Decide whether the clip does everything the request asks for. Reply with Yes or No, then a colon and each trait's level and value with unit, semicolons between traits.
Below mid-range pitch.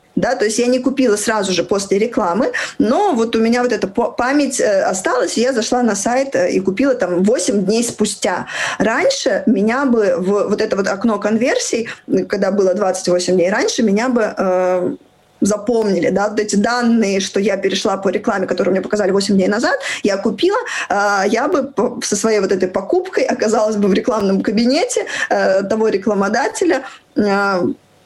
No: high, 215 Hz